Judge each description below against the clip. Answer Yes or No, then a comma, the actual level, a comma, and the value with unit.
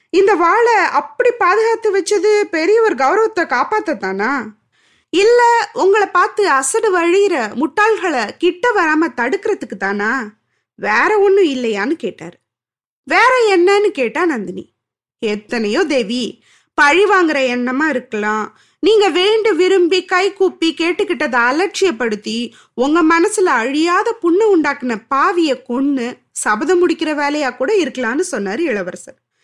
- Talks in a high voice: Yes, very high, 345 Hz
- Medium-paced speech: Yes, average, 110 wpm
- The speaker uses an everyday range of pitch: No, wide, 7.7 semitones